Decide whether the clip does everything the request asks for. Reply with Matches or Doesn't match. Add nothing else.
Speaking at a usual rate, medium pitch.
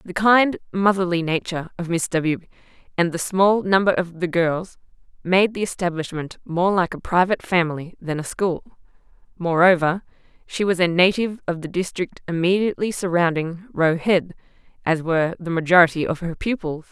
Matches